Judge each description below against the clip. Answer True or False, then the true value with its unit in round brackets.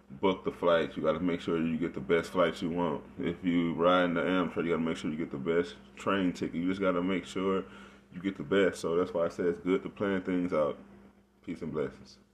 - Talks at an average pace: False (270 wpm)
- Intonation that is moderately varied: False (1.9 semitones)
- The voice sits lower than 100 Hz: True (90 Hz)